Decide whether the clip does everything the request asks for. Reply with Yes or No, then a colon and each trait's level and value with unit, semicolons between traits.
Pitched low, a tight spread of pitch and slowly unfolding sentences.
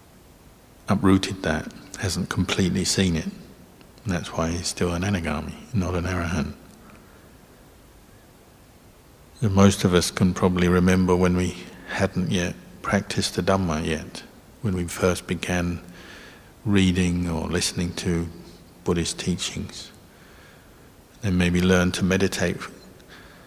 Yes: very low, 90 Hz; narrow, 1.5 semitones; slow, 120 wpm